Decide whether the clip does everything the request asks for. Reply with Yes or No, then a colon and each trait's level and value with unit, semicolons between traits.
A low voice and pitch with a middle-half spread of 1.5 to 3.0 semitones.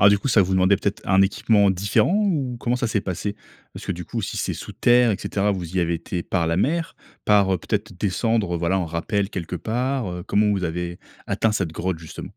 No: low, 100 Hz; average, 3.8 semitones